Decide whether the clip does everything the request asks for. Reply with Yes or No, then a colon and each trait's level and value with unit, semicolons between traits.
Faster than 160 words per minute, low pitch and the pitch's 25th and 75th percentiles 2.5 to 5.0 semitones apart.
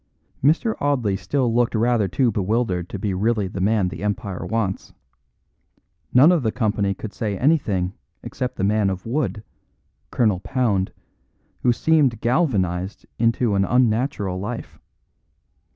No: slow, 135 wpm; low, 110 Hz; average, 4.2 semitones